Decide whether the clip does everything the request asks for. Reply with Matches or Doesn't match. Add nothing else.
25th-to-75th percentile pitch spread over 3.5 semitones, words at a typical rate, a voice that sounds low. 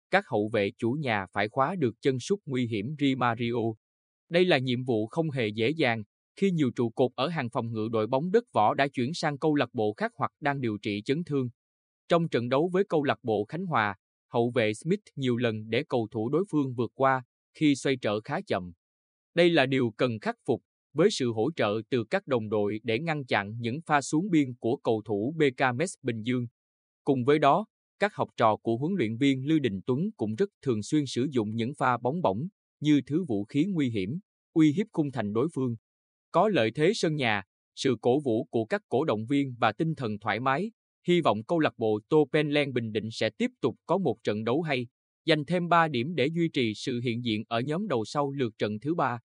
Matches